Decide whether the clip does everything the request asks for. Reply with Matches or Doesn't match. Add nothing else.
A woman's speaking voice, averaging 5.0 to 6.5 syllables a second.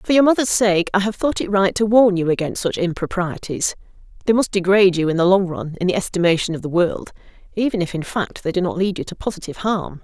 Matches